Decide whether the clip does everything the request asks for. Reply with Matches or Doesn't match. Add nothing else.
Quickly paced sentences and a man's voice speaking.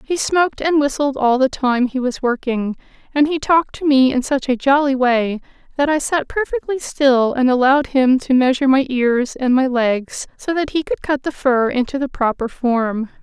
Doesn't match